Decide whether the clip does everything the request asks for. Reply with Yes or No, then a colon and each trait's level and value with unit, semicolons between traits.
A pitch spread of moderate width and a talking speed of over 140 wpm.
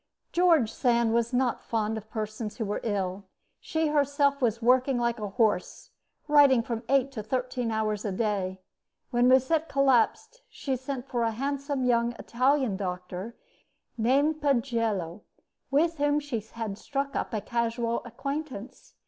Yes: average, 4.0 semitones; average, 150 wpm